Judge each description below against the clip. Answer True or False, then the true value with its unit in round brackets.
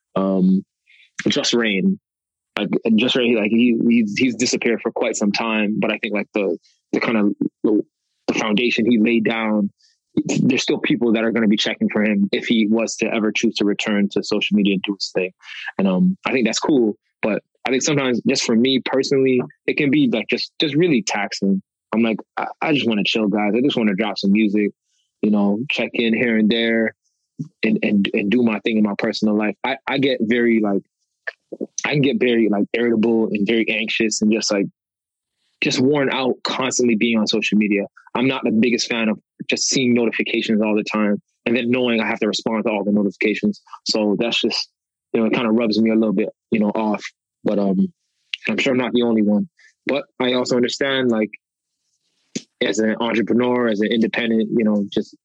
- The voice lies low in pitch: True (110 Hz)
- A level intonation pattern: True (2.2 semitones)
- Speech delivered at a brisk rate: True (215 wpm)